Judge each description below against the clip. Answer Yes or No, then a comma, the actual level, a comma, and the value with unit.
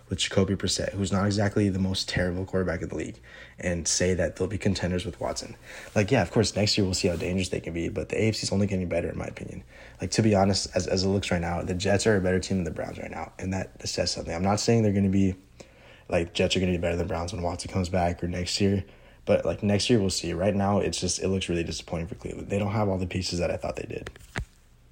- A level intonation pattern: Yes, narrow, 2.1 semitones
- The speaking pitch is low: Yes, very low, 95 Hz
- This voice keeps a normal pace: No, fast, 285 wpm